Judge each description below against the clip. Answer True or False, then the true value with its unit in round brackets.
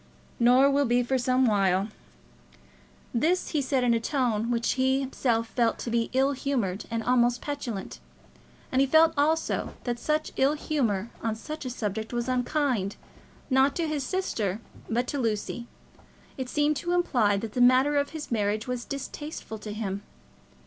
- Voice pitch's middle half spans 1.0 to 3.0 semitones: False (3.8 semitones)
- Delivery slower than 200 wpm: True (170 wpm)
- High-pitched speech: True (250 Hz)